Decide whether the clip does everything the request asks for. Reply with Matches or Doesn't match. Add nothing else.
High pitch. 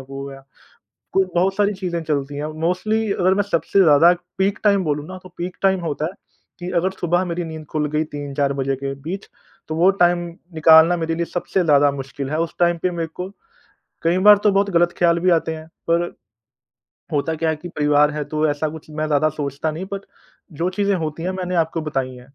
Doesn't match